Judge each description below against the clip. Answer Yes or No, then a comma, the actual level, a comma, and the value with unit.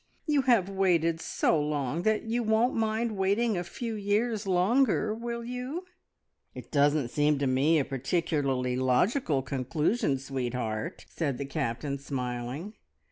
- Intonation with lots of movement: Yes, wide, 8.2 semitones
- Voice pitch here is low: No, medium, 165 Hz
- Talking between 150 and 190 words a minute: No, slow, 135 wpm